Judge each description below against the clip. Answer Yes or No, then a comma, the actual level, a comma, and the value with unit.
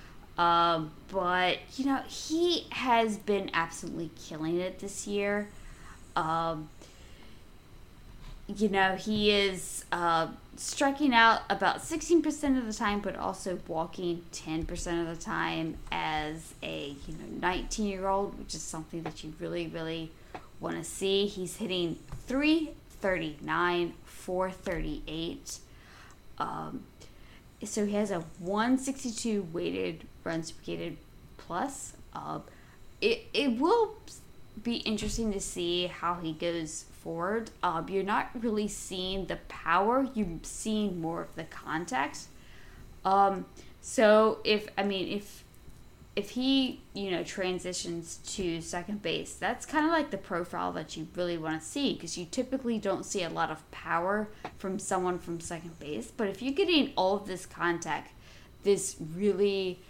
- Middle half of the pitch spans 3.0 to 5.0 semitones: Yes, average, 4.2 semitones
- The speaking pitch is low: No, high, 190 Hz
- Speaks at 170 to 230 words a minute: No, slow, 135 wpm